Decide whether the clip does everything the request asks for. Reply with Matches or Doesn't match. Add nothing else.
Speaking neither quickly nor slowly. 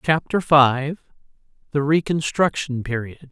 Doesn't match